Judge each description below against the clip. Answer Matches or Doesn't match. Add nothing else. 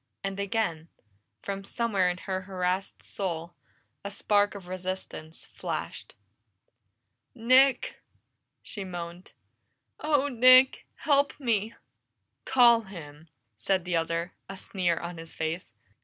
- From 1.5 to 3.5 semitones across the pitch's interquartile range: Doesn't match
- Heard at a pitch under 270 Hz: Matches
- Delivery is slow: Matches